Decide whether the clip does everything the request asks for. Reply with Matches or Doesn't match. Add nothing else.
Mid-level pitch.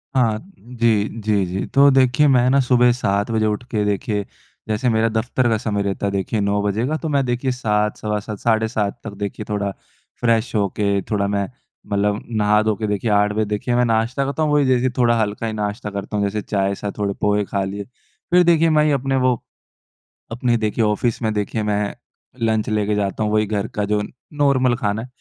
Doesn't match